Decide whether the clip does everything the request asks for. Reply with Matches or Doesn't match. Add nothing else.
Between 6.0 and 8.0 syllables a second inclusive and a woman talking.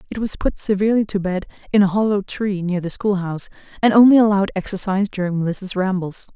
Matches